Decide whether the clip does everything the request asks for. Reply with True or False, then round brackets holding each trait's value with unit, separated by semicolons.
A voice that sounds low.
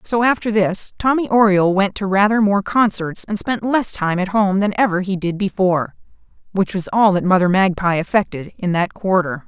False (195 Hz)